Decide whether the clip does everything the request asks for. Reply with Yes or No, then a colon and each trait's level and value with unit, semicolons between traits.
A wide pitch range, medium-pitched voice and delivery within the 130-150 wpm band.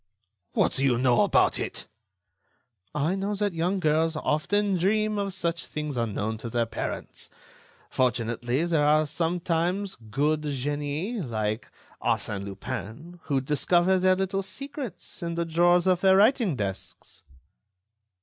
Yes: wide, 6.3 semitones; medium, 165 Hz; slow, 135 wpm